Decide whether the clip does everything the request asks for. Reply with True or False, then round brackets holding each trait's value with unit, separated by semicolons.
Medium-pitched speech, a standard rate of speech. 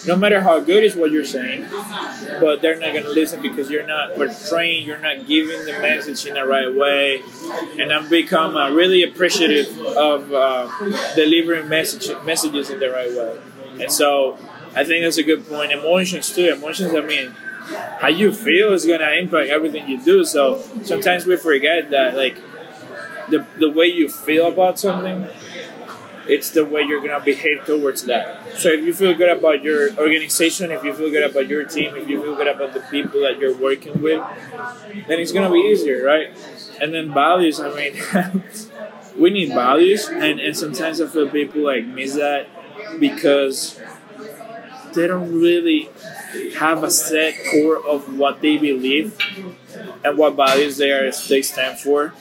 True (160 Hz; 175 wpm)